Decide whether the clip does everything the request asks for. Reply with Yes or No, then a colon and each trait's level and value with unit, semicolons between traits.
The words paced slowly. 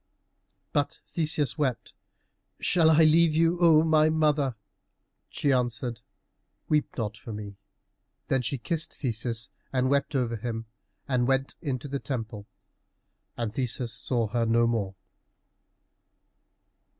Yes: slow, 125 wpm